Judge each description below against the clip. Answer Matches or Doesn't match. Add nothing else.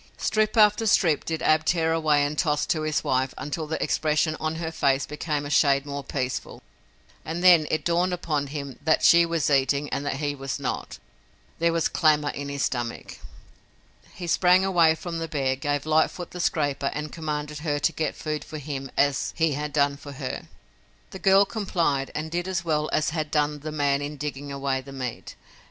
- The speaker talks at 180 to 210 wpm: Matches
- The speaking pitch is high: Doesn't match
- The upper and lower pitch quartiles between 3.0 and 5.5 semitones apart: Doesn't match